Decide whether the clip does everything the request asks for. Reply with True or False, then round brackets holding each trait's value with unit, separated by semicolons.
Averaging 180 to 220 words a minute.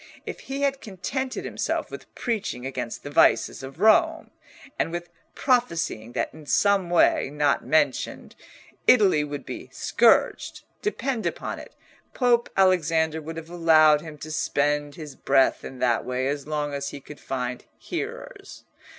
False (150 wpm)